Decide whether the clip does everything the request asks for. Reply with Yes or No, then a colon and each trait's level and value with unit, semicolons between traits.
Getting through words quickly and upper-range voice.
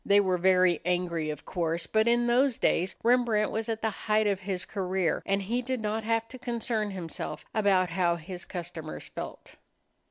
No: average, 185 wpm; high, 200 Hz